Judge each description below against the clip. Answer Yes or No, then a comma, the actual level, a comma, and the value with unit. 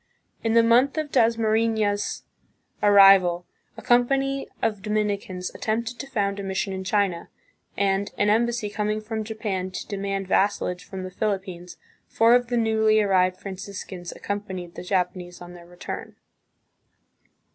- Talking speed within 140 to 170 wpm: Yes, average, 145 wpm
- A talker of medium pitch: No, high, 205 Hz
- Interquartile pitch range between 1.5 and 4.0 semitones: Yes, average, 3.0 semitones